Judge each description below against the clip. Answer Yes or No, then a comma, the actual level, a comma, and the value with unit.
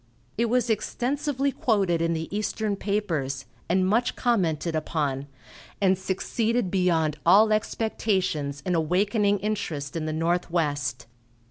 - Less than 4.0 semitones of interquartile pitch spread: No, average, 5.2 semitones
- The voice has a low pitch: No, medium, 185 Hz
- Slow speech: Yes, slow, 120 wpm